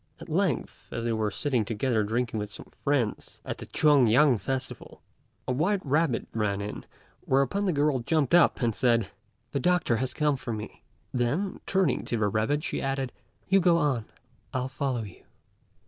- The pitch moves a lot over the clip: No, average, 4.7 semitones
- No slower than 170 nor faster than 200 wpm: Yes, average, 180 wpm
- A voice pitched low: Yes, low, 130 Hz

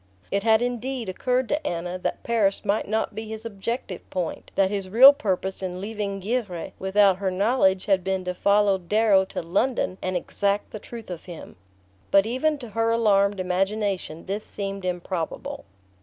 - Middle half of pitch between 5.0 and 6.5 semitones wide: No, average, 3.0 semitones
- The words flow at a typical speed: Yes, average, 170 wpm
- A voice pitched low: No, high, 200 Hz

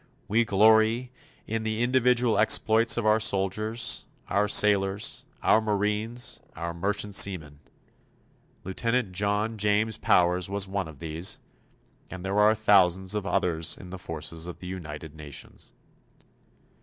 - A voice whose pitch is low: Yes, low, 100 Hz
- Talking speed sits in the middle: No, slow, 130 wpm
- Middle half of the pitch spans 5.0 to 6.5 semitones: No, average, 3.4 semitones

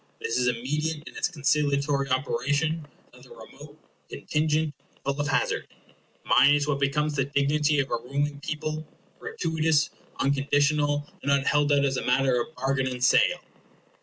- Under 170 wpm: Yes, average, 160 wpm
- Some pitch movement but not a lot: No, narrow, 1.8 semitones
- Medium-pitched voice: Yes, medium, 145 Hz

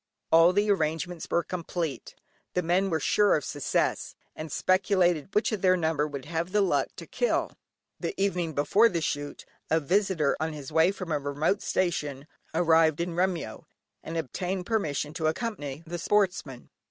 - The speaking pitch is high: No, medium, 170 Hz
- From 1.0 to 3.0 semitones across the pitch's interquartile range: No, average, 3.4 semitones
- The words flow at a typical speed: Yes, average, 165 wpm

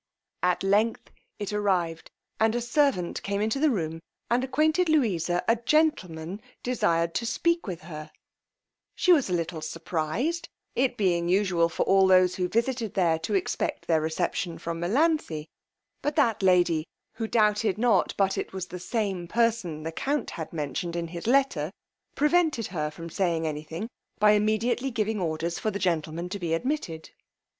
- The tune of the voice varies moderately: No, wide, 5.7 semitones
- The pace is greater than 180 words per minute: No, average, 165 wpm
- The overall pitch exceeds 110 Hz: Yes, high, 190 Hz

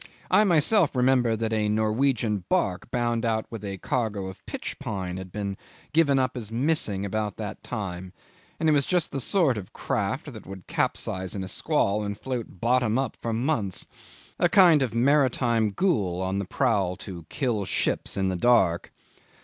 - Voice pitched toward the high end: No, low, 110 Hz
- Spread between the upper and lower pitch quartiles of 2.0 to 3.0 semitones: No, average, 5.1 semitones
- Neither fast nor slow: Yes, average, 180 wpm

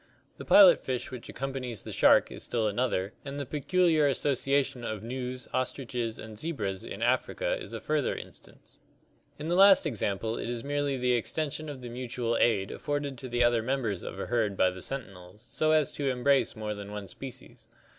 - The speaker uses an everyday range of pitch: Yes, average, 4.1 semitones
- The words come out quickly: Yes, fast, 215 wpm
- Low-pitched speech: Yes, low, 125 Hz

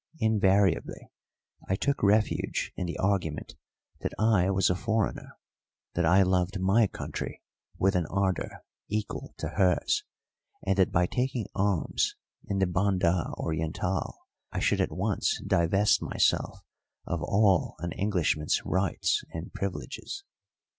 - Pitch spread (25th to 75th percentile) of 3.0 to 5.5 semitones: No, narrow, 2.4 semitones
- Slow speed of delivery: Yes, slow, 130 wpm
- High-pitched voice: No, very low, 95 Hz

